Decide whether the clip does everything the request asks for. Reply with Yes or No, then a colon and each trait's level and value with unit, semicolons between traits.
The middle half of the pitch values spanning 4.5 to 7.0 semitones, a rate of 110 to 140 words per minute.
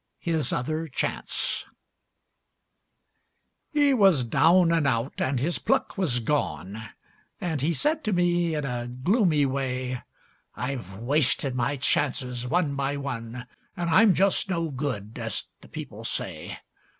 Yes: average, 5.3 semitones; slow, 135 wpm